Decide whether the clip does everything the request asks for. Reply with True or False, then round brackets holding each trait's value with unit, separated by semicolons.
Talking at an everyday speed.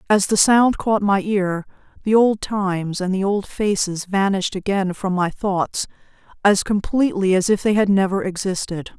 True (175 wpm)